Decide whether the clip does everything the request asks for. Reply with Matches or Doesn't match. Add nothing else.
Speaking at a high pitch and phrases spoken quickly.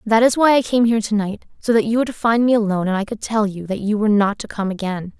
Matches